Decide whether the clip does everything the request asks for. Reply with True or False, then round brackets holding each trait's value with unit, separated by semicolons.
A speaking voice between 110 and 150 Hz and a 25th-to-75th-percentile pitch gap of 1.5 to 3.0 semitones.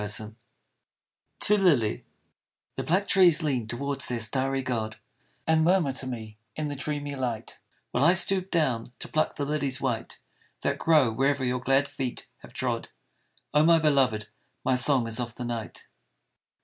False (135 Hz; 4.2 semitones)